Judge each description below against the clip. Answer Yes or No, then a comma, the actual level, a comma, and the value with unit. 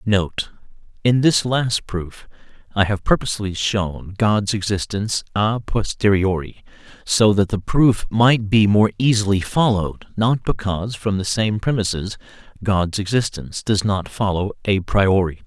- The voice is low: Yes, low, 105 Hz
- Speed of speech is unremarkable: No, slow, 130 wpm